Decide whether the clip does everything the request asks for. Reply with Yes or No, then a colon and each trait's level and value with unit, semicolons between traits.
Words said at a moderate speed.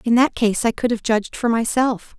No: fast, 250 wpm